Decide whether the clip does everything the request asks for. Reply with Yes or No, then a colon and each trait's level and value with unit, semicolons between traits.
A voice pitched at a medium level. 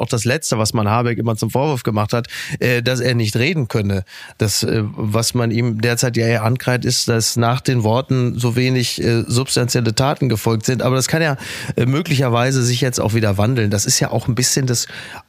No: low, 120 Hz